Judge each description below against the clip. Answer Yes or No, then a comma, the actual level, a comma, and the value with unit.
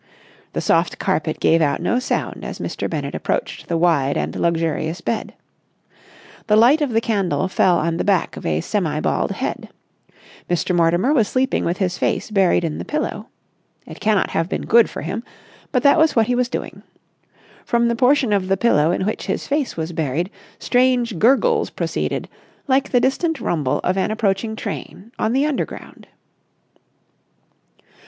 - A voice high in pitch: Yes, high, 210 Hz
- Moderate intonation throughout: No, wide, 6.5 semitones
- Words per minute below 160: No, average, 175 wpm